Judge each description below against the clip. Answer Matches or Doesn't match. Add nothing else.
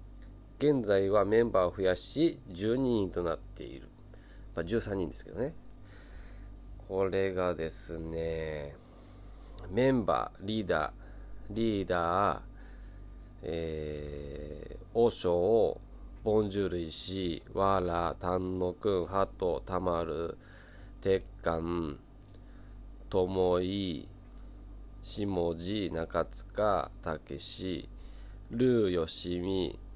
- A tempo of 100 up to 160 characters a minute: Matches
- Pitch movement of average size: Matches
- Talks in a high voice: Doesn't match